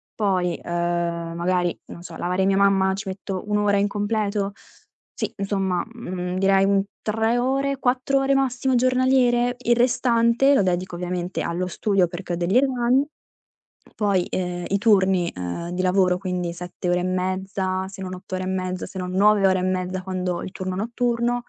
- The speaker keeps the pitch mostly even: No, average, 4.0 semitones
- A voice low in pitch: No, high, 190 Hz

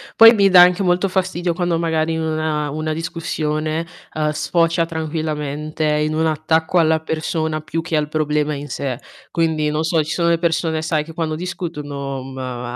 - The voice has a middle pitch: Yes, medium, 160 Hz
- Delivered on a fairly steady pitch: Yes, narrow, 1.6 semitones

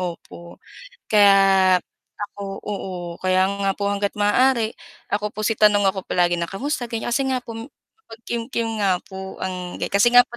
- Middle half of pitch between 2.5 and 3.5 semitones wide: Yes, average, 3.1 semitones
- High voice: Yes, high, 200 Hz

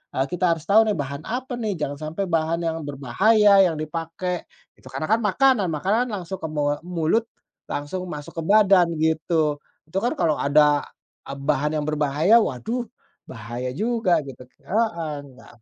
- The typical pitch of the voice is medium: Yes, medium, 165 Hz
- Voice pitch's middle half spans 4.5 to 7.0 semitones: Yes, wide, 5.5 semitones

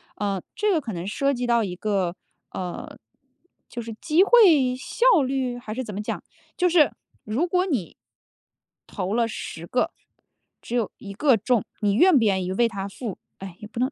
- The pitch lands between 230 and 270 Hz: Yes, high, 235 Hz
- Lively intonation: Yes, wide, 5.8 semitones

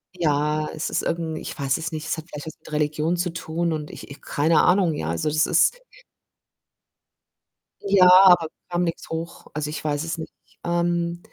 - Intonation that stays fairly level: Yes, narrow, 2.2 semitones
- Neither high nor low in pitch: Yes, medium, 160 Hz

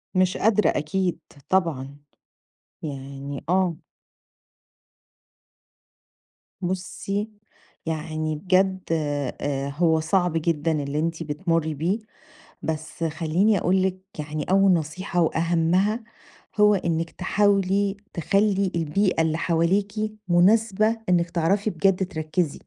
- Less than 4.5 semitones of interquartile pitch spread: Yes, average, 3.5 semitones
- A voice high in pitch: No, medium, 170 Hz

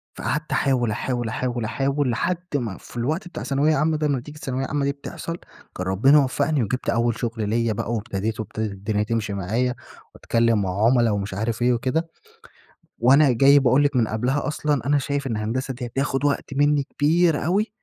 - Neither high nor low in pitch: No, low, 125 Hz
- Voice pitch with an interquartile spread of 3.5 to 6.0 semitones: Yes, average, 4.2 semitones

